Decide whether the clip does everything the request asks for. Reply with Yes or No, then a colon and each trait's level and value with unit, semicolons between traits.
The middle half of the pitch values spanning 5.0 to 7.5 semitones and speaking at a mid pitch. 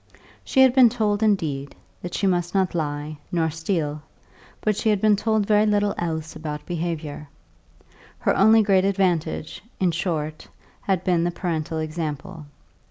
No: average, 4.5 semitones; medium, 175 Hz